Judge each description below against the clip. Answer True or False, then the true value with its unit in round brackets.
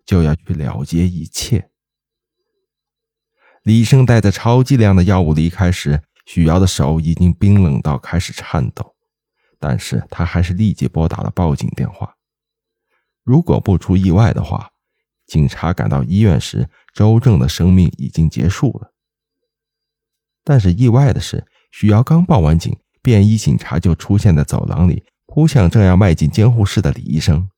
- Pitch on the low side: True (95 Hz)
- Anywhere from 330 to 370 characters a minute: False (235 characters per minute)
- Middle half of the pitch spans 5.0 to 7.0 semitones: True (5.5 semitones)